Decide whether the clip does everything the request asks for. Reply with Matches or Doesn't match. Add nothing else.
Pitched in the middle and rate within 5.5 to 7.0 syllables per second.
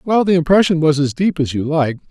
Matches